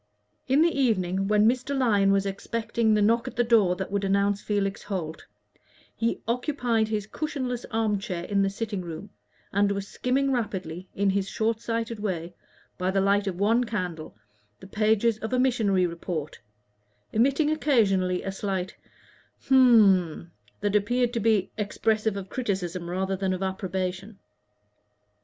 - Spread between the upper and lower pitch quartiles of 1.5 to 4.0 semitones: Yes, average, 3.4 semitones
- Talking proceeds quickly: No, average, 155 wpm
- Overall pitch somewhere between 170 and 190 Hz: No, high, 205 Hz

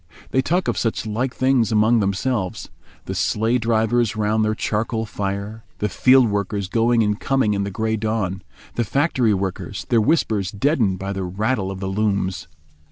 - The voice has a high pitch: No, low, 110 Hz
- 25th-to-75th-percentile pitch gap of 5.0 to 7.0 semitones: No, average, 2.9 semitones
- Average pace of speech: Yes, average, 170 wpm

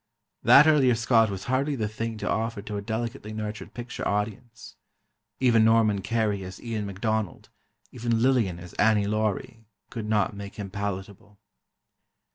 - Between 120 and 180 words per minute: Yes, average, 150 wpm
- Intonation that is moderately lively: No, narrow, 2.1 semitones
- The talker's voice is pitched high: No, low, 110 Hz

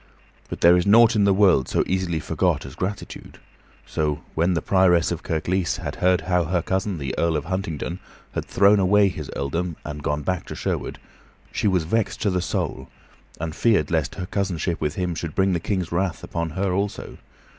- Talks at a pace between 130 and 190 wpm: No, average, 200 wpm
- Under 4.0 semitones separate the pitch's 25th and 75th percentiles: Yes, average, 3.0 semitones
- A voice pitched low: Yes, very low, 90 Hz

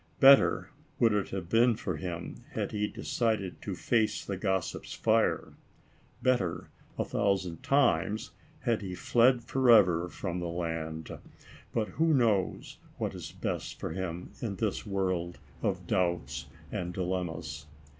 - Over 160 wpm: No, average, 145 wpm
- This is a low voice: Yes, very low, 95 Hz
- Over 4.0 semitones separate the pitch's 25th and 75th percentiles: Yes, average, 4.6 semitones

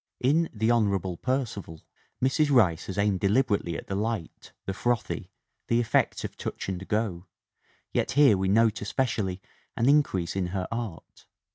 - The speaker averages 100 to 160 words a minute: Yes, average, 155 wpm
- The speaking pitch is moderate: No, low, 105 Hz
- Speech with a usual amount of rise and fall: Yes, average, 4.1 semitones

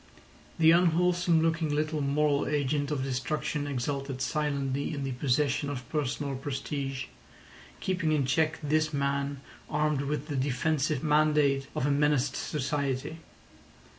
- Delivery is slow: Yes, slow, 130 wpm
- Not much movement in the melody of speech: Yes, narrow, 2.0 semitones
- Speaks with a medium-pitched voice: Yes, medium, 145 Hz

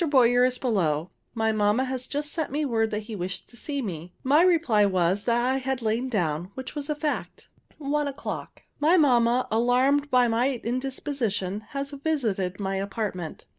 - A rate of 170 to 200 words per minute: Yes, average, 175 wpm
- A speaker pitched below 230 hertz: No, high, 245 Hz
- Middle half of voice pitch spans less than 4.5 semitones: No, average, 5.0 semitones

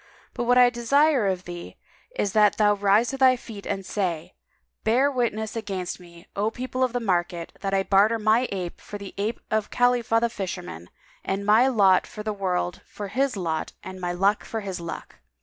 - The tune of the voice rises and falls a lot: No, average, 4.0 semitones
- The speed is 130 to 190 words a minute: No, average, 200 wpm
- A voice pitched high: Yes, high, 205 Hz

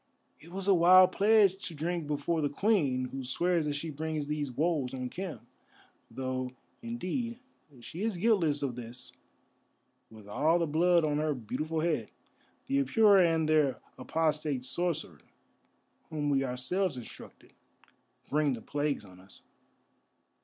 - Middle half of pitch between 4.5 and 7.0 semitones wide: Yes, average, 4.8 semitones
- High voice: No, medium, 155 Hz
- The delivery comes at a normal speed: Yes, average, 145 wpm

